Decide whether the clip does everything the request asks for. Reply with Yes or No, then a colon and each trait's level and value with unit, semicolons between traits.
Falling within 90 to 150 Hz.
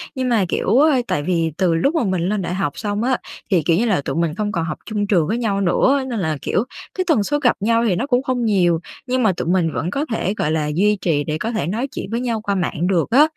No: high, 200 Hz